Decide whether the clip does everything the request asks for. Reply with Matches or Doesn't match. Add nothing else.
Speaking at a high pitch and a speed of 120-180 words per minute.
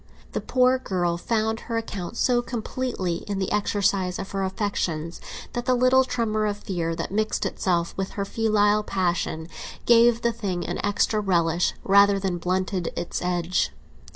Matches